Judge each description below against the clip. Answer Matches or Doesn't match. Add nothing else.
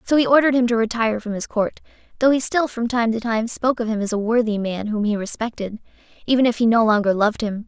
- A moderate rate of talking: Doesn't match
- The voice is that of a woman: Matches